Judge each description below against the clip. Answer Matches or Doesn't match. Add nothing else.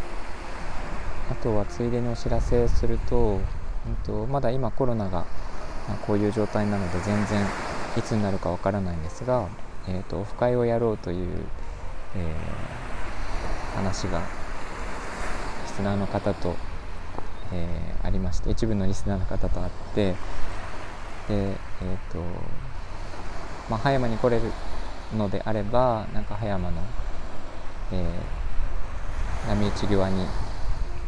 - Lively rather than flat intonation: Doesn't match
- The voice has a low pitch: Matches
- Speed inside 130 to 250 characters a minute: Matches